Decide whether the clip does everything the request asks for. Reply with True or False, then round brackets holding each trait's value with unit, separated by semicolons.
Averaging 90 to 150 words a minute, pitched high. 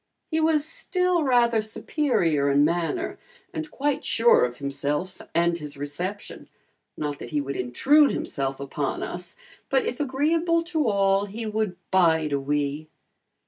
True (145 wpm; 195 Hz)